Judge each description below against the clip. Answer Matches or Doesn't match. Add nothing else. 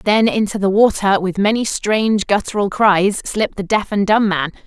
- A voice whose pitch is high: Matches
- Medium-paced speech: Matches